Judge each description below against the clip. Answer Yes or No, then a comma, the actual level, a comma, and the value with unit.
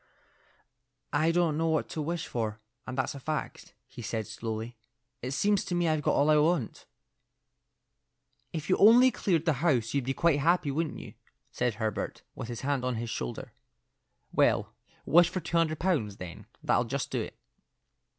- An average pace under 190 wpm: Yes, average, 180 wpm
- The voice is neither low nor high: Yes, medium, 145 Hz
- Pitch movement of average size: No, wide, 5.8 semitones